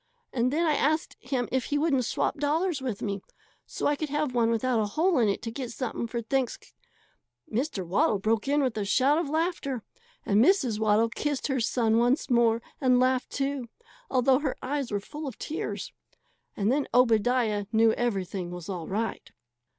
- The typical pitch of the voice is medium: No, very high, 250 Hz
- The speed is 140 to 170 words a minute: No, average, 190 wpm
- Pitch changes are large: No, average, 4.3 semitones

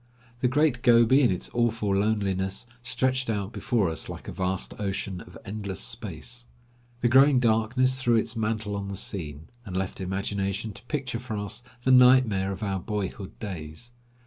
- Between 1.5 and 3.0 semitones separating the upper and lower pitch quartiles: No, average, 4.0 semitones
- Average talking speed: Yes, average, 170 wpm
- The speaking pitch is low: Yes, low, 110 Hz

